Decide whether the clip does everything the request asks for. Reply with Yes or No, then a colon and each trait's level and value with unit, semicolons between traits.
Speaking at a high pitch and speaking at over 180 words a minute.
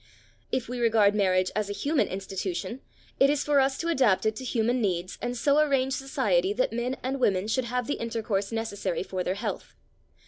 Yes: high, 230 Hz; average, 200 wpm